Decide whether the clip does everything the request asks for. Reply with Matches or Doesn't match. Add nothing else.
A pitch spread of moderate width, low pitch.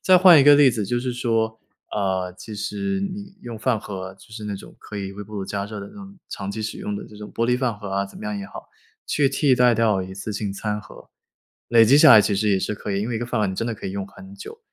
Matches